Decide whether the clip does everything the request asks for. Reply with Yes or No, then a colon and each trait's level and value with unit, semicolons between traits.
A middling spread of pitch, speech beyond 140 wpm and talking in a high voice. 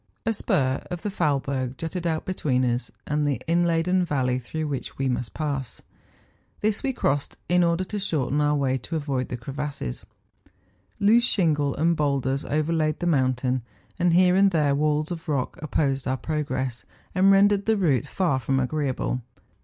No: average, 4.5 semitones; average, 165 wpm; medium, 150 Hz